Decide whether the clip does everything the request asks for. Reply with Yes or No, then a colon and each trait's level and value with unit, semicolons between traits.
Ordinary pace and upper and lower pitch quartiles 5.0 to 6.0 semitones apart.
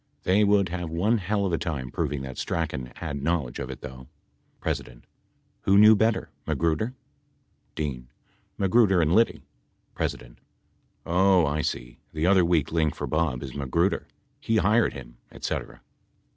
Yes: average, 155 wpm; wide, 5.6 semitones